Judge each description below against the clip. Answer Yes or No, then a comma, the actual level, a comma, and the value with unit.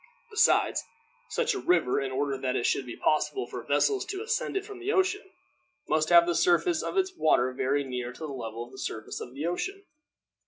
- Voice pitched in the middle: Yes, medium, 160 Hz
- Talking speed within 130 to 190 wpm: No, fast, 205 wpm